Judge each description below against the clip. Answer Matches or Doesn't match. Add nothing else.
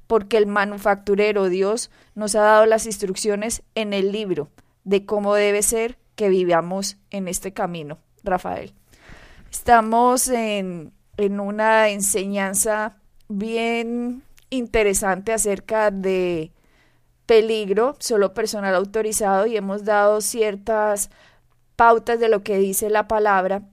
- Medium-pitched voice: Doesn't match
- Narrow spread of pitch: Matches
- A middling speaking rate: Doesn't match